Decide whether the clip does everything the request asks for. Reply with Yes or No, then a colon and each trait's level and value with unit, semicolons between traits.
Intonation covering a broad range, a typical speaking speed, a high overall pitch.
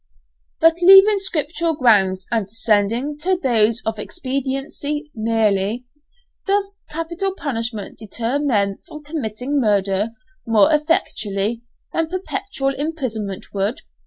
No: wide, 6.8 semitones; slow, 105 wpm; very high, 260 Hz